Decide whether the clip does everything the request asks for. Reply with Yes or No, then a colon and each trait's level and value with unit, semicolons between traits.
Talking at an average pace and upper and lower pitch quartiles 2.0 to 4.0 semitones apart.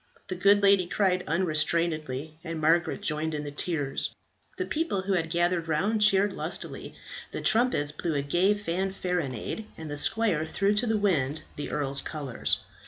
No: average, 165 wpm; average, 4.6 semitones